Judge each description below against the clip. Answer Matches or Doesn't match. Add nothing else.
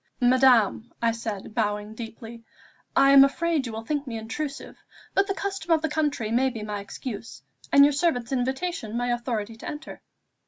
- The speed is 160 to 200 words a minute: Matches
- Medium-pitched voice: Doesn't match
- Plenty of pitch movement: Doesn't match